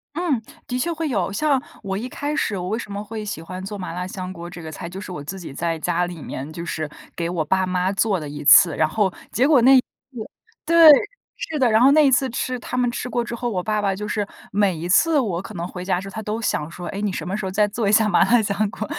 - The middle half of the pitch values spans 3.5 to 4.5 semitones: No, average, 5.0 semitones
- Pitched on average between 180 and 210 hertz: Yes, high, 200 Hz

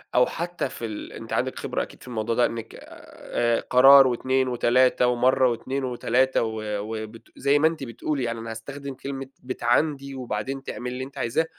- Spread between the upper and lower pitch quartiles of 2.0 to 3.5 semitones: Yes, narrow, 2.6 semitones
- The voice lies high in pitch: No, low, 125 Hz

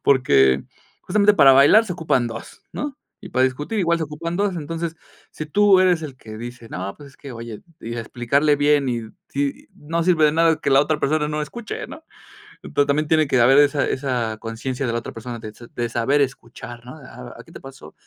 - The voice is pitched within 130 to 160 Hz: Yes, medium, 140 Hz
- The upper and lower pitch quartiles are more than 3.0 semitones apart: Yes, average, 4.7 semitones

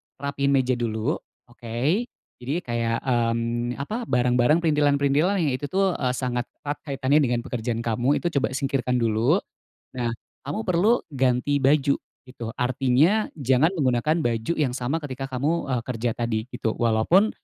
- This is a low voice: Yes, low, 130 Hz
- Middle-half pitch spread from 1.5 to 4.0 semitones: Yes, average, 3.5 semitones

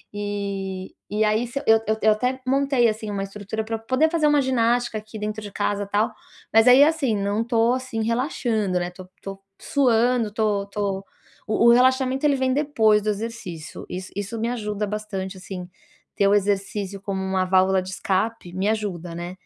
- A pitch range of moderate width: Yes, average, 3.2 semitones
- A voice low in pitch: No, high, 215 Hz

